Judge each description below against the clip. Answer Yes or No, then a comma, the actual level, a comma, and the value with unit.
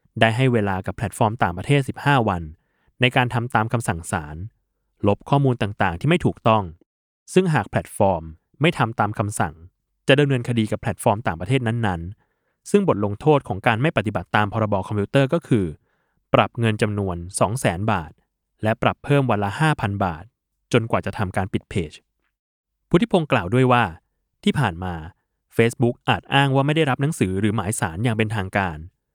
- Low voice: Yes, low, 110 Hz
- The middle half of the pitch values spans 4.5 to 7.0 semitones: Yes, average, 4.9 semitones